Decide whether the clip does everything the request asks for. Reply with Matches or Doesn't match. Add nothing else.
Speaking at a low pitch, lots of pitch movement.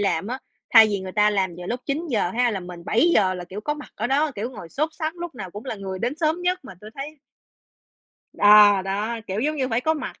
Doesn't match